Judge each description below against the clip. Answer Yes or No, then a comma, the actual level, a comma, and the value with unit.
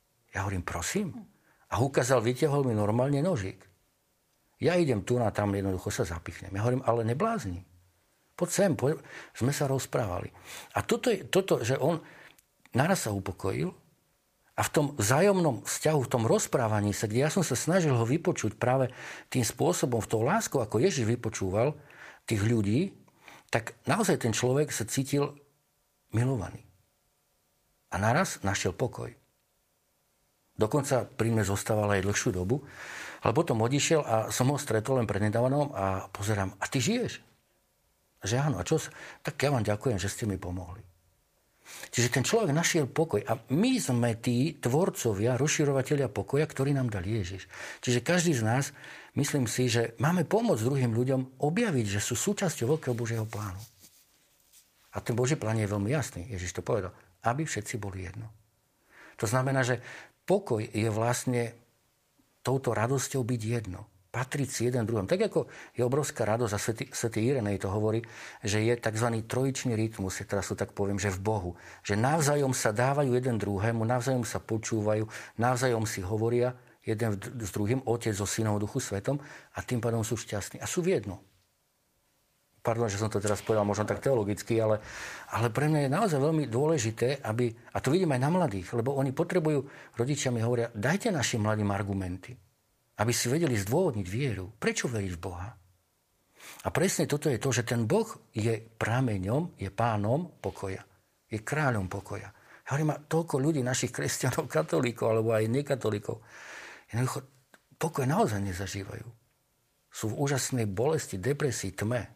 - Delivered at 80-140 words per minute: No, average, 160 wpm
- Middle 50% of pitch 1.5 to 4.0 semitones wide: No, average, 4.8 semitones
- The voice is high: No, low, 120 Hz